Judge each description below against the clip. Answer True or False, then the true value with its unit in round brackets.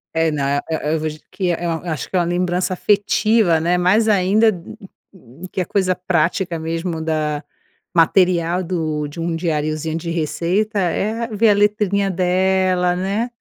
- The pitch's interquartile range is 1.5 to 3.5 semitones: True (2.9 semitones)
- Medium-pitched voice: True (180 Hz)